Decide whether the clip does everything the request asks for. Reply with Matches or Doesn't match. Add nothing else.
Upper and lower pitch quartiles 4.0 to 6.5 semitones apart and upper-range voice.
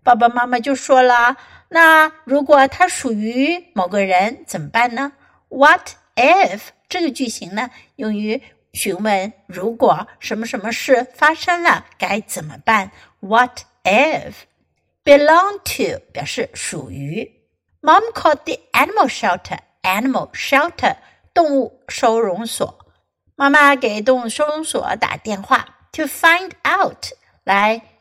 Matches